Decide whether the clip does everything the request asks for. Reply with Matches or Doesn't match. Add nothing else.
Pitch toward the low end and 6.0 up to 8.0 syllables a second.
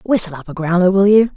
Doesn't match